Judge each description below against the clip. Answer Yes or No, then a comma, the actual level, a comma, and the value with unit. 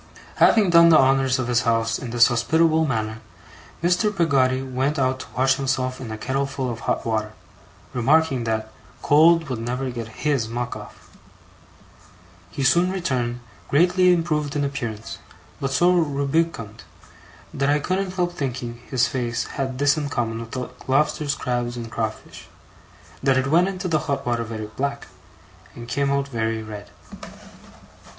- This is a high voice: No, low, 130 Hz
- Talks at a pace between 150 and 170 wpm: Yes, average, 160 wpm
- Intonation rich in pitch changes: No, average, 4.3 semitones